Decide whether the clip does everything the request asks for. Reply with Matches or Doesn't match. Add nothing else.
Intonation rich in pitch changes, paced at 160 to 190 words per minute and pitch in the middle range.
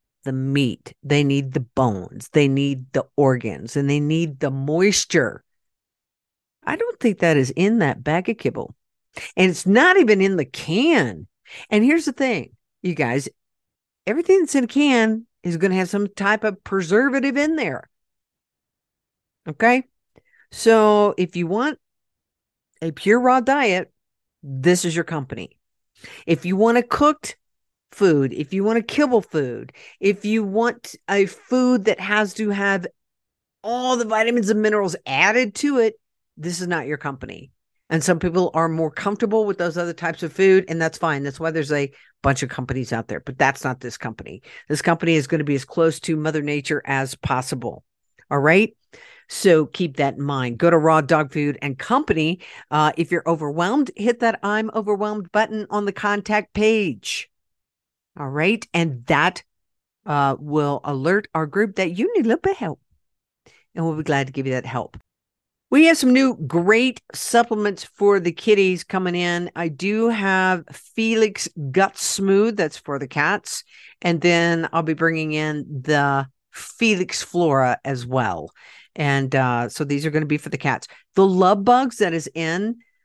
Matches